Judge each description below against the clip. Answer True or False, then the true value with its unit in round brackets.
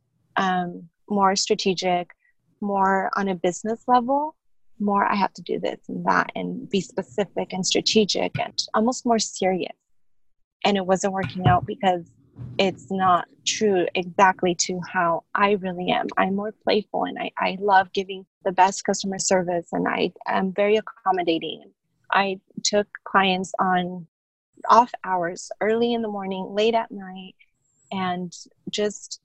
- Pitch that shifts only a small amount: True (2.3 semitones)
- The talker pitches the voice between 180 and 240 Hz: True (190 Hz)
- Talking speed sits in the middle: True (150 wpm)